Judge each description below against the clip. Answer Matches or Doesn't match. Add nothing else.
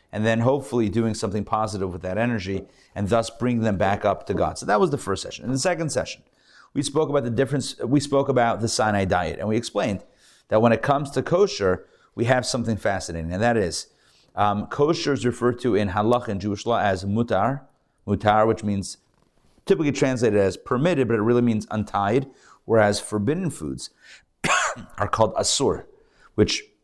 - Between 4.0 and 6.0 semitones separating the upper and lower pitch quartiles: Matches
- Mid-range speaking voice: Doesn't match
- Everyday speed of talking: Matches